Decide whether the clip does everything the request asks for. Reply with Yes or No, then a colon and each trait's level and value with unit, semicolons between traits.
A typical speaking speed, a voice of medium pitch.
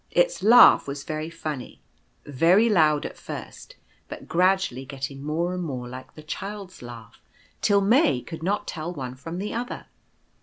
Yes: average, 160 wpm; medium, 160 Hz